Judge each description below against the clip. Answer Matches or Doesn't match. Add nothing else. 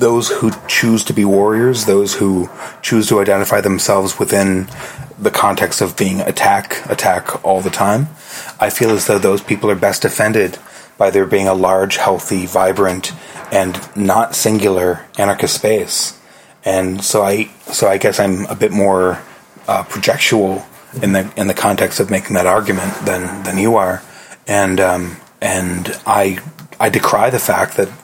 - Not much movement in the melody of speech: Matches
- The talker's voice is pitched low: Matches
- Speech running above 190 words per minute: Doesn't match